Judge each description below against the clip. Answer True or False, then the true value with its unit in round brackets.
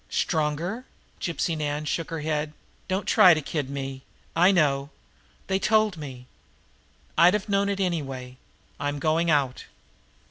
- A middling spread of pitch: True (4.1 semitones)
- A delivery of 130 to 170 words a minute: True (140 wpm)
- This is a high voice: False (155 Hz)